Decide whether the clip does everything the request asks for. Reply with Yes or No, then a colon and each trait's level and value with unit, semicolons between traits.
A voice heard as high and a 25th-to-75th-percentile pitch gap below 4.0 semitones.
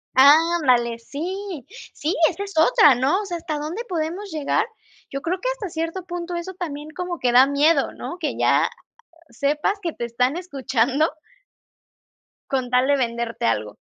No: very high, 310 Hz; average, 5.2 semitones